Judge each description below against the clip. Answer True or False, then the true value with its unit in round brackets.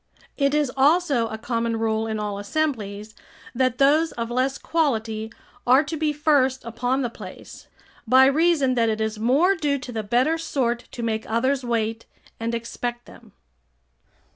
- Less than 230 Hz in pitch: False (245 Hz)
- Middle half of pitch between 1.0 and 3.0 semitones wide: False (3.8 semitones)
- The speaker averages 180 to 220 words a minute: False (165 wpm)